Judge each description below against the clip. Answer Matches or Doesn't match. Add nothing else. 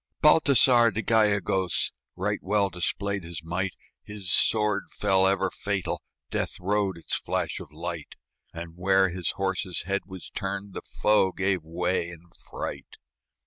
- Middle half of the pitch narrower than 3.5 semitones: Matches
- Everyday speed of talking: Matches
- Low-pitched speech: Matches